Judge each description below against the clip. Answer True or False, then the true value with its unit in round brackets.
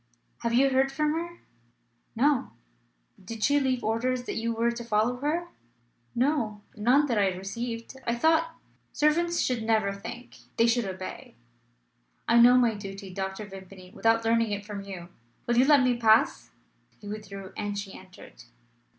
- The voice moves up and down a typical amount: True (4.0 semitones)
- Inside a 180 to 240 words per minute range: False (165 wpm)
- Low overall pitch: False (230 Hz)